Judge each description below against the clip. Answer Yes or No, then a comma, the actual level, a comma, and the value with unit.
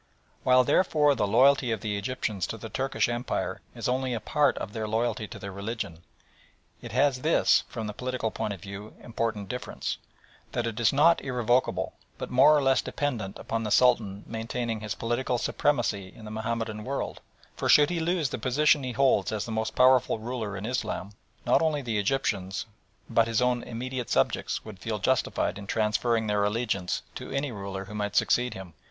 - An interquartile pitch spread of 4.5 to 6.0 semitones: No, average, 3.4 semitones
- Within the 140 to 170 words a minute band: No, average, 190 wpm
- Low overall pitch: Yes, low, 115 Hz